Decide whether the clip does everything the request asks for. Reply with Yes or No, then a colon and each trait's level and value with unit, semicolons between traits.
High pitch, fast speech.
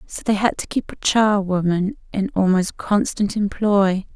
No: high, 200 Hz; average, 160 wpm